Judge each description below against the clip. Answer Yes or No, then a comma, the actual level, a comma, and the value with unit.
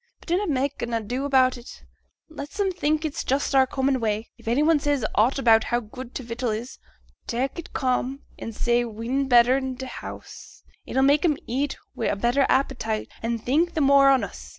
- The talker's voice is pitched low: No, very high, 260 Hz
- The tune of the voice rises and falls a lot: No, average, 3.0 semitones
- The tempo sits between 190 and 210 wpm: Yes, fast, 205 wpm